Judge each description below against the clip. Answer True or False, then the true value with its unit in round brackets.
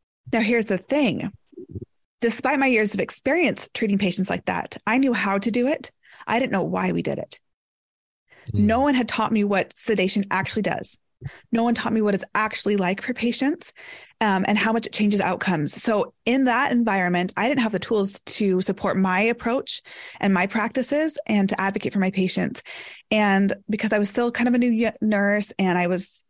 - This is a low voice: False (215 Hz)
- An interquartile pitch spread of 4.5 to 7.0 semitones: False (3.6 semitones)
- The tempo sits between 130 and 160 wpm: False (200 wpm)